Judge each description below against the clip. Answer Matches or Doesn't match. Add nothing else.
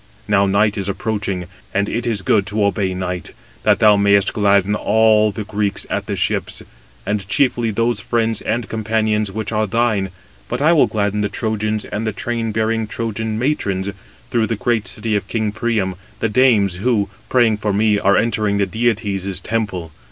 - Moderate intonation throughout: Doesn't match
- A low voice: Matches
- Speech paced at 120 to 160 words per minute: Doesn't match